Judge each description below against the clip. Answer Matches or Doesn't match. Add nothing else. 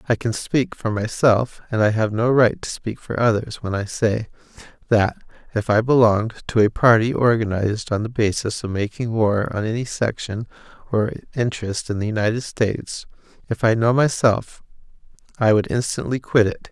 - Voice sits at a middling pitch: Doesn't match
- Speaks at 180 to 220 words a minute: Doesn't match